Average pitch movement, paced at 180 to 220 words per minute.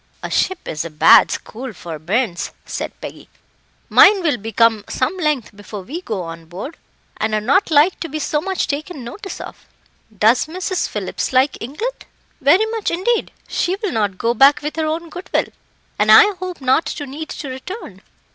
No: wide, 8.3 semitones; average, 185 wpm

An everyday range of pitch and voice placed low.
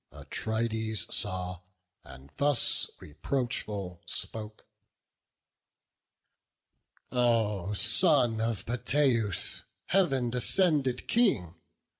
Yes: average, 4.4 semitones; low, 115 Hz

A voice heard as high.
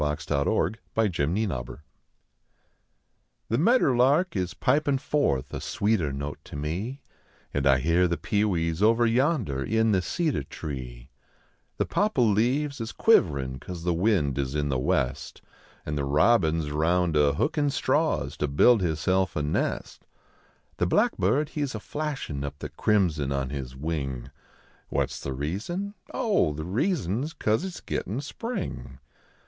No: very low, 90 Hz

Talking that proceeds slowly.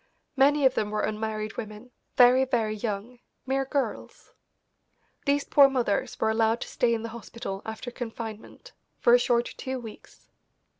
No: average, 155 wpm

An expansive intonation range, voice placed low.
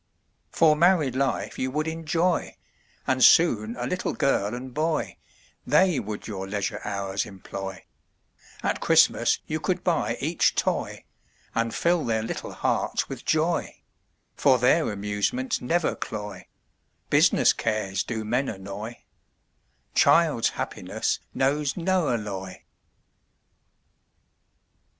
Yes: wide, 7.3 semitones; low, 125 Hz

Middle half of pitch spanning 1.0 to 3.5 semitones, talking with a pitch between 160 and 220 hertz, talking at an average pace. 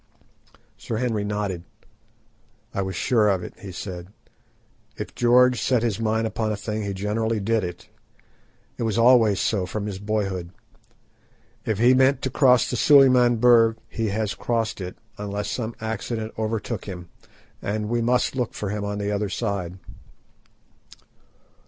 No: average, 2.7 semitones; low, 110 Hz; average, 155 wpm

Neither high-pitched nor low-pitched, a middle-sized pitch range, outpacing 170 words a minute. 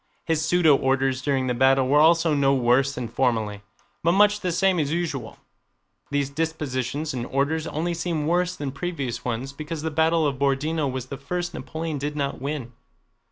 Yes: medium, 145 Hz; average, 3.4 semitones; average, 180 wpm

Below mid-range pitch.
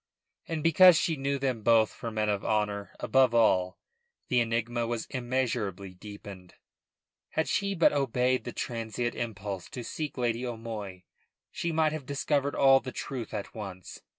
Yes: low, 120 Hz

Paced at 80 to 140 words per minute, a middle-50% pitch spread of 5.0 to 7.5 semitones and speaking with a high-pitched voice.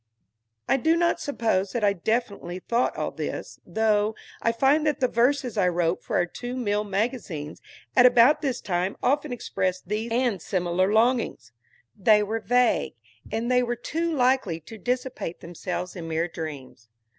No: average, 165 wpm; average, 5.3 semitones; high, 220 Hz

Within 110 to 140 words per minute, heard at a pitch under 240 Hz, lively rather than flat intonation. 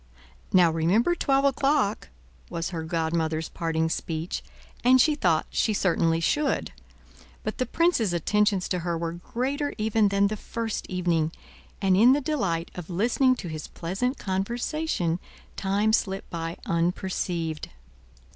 Yes: slow, 135 wpm; high, 190 Hz; wide, 6.2 semitones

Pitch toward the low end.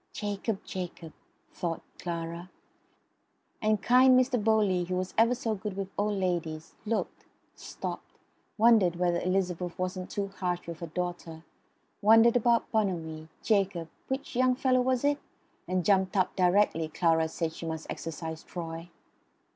No: medium, 185 Hz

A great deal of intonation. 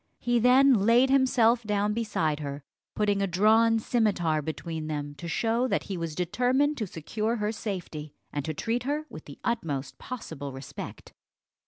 Yes: wide, 7.0 semitones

